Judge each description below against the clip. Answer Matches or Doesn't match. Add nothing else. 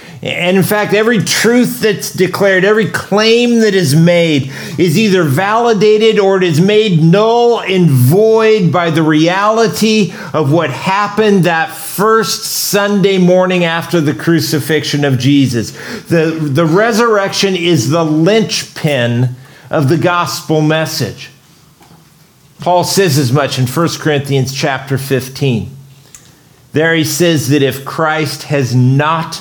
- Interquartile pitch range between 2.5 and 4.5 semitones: Doesn't match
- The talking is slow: Matches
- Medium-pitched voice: Matches